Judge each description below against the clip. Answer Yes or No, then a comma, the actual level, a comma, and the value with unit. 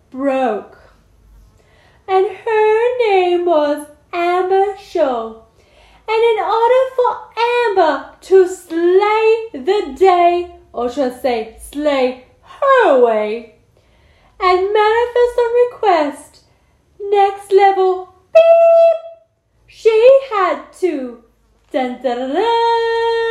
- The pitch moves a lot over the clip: Yes, wide, 7.2 semitones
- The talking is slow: Yes, slow, 95 wpm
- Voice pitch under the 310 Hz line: No, very high, 365 Hz